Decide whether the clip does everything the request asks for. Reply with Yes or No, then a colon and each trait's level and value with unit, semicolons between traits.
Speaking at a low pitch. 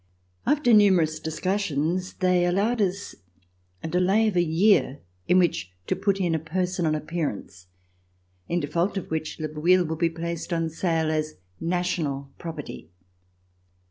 No: medium, 170 Hz